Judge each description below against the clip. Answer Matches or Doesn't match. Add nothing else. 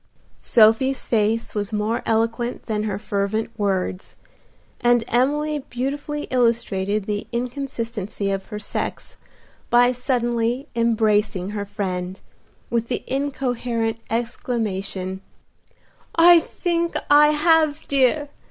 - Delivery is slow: Matches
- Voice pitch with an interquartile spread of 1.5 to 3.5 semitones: Doesn't match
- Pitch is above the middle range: Matches